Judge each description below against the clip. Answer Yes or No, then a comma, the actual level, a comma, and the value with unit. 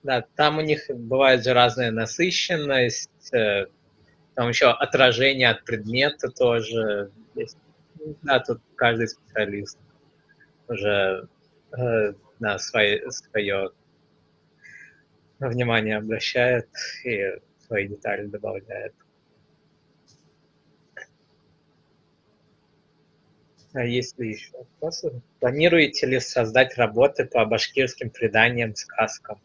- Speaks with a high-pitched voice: No, low, 120 Hz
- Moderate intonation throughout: Yes, average, 3.4 semitones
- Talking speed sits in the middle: No, slow, 85 wpm